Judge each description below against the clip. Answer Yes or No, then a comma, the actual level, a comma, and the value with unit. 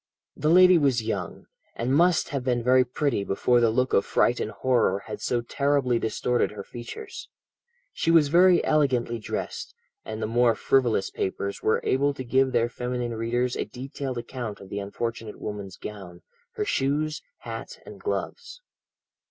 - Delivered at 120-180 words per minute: Yes, average, 165 wpm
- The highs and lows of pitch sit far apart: No, average, 3.9 semitones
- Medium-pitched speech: No, low, 125 Hz